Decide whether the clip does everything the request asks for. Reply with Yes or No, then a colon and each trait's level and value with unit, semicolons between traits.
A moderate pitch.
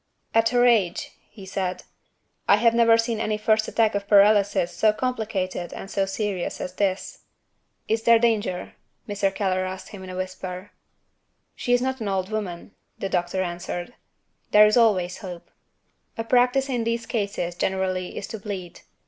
No: high, 205 Hz